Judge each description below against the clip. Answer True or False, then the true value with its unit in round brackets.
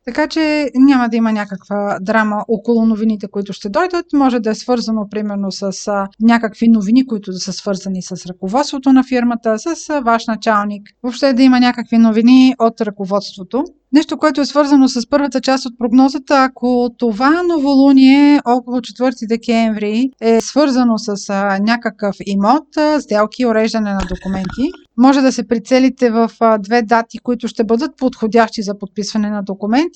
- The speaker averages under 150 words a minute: False (155 wpm)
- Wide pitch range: False (3.8 semitones)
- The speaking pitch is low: False (235 Hz)